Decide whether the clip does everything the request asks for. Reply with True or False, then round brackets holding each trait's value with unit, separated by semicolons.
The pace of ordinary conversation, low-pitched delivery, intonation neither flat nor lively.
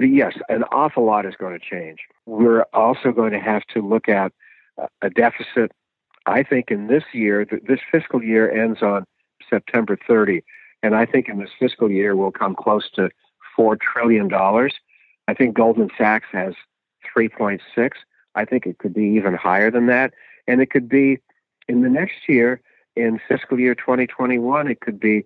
True (175 wpm; 115 Hz; 3.0 semitones)